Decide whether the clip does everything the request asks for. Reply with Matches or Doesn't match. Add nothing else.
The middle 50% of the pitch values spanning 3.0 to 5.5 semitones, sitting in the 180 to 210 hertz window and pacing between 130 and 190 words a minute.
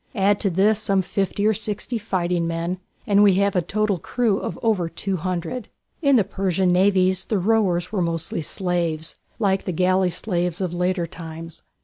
Doesn't match